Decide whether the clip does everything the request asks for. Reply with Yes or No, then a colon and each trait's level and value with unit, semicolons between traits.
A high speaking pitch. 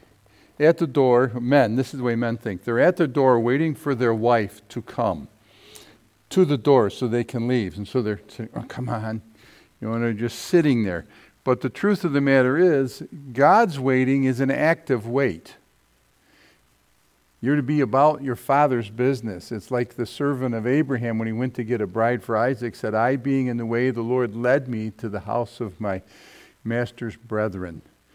No: low, 125 Hz